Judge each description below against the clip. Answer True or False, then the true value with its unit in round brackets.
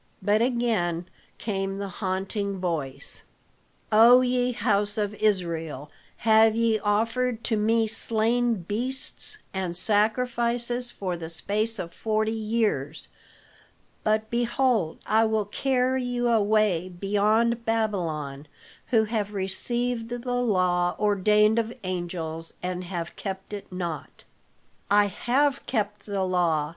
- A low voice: False (210 Hz)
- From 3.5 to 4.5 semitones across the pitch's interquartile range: True (4.0 semitones)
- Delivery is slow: True (120 wpm)